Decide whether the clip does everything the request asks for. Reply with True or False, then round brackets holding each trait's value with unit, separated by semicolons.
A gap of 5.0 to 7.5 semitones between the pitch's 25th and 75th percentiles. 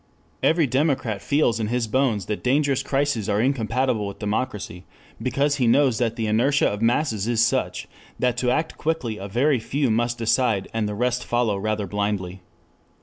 False (3.9 semitones)